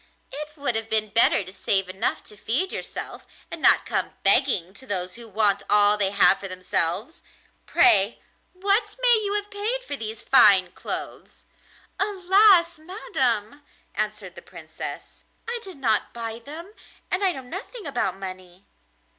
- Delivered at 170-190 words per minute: No, average, 155 wpm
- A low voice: No, high, 240 Hz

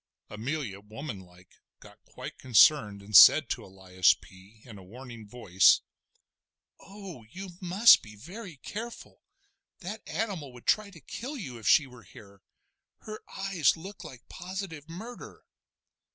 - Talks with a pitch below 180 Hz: Yes, low, 135 Hz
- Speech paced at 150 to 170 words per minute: No, slow, 135 wpm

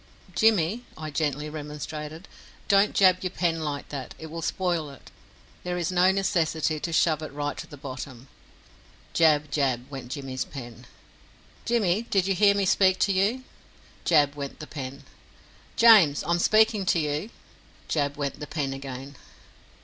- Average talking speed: Yes, average, 160 wpm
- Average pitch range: Yes, average, 4.5 semitones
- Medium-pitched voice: Yes, medium, 155 Hz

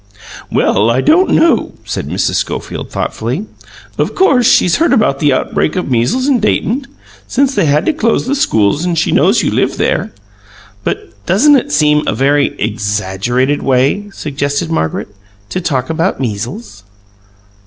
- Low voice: No, medium, 145 Hz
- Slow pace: No, average, 160 wpm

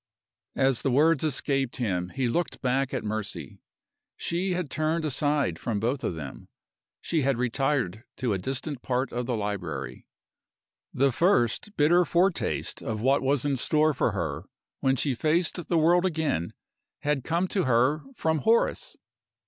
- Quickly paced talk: No, average, 155 wpm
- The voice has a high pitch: No, low, 135 Hz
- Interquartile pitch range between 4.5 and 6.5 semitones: Yes, average, 4.9 semitones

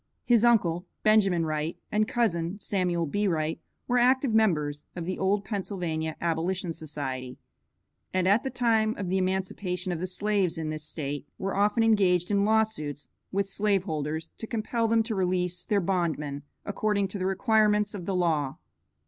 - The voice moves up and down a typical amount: Yes, average, 4.3 semitones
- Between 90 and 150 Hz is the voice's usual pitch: No, high, 190 Hz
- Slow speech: No, average, 165 wpm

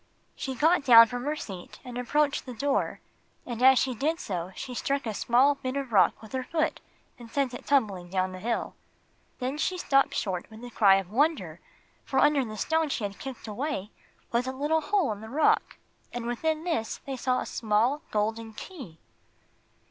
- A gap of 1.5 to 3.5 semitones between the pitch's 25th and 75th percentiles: No, average, 4.6 semitones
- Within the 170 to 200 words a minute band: Yes, average, 195 wpm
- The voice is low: No, very high, 250 Hz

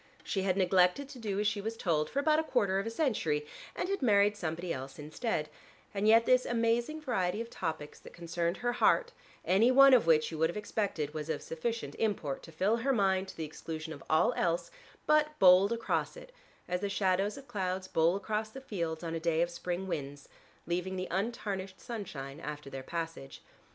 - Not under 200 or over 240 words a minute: Yes, fast, 205 wpm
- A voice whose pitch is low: No, high, 190 Hz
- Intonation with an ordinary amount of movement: No, wide, 5.7 semitones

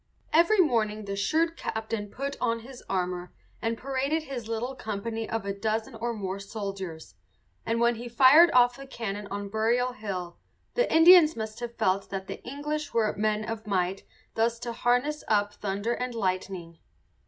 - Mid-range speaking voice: No, high, 225 Hz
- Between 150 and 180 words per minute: Yes, average, 170 wpm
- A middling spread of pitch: Yes, average, 3.8 semitones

